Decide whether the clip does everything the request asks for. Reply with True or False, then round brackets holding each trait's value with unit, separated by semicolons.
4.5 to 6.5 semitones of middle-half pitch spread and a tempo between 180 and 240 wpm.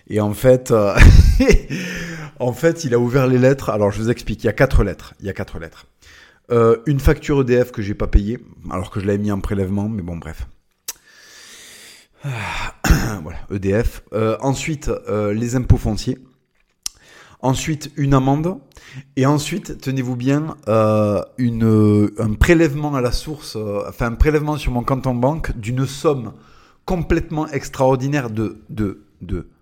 False (4.8 semitones; 170 wpm)